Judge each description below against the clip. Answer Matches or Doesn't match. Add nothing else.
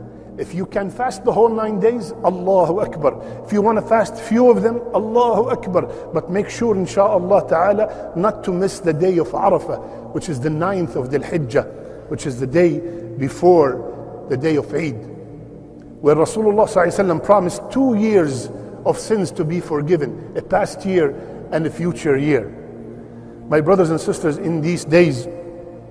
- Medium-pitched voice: Matches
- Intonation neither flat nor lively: Matches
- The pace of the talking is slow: Doesn't match